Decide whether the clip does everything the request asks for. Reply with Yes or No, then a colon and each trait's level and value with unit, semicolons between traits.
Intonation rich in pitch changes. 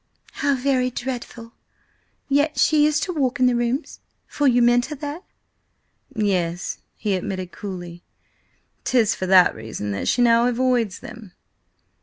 Yes: wide, 5.9 semitones